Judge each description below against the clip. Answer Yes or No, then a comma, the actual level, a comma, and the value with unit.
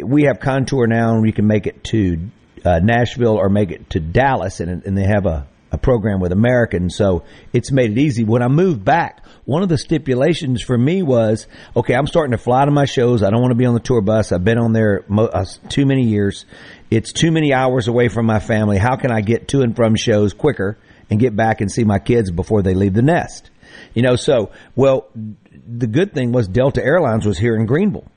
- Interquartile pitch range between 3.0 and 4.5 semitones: Yes, average, 3.5 semitones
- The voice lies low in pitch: Yes, low, 115 Hz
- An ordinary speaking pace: No, fast, 235 wpm